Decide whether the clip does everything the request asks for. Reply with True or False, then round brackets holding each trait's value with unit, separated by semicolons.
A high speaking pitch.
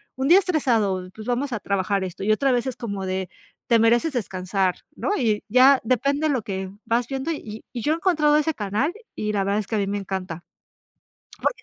True (225 Hz)